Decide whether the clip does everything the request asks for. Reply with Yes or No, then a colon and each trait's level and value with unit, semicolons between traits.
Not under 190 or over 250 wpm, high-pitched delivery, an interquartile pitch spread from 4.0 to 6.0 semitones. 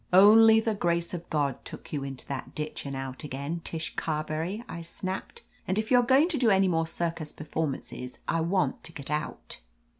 No: average, 200 wpm; medium, 165 Hz; average, 4.4 semitones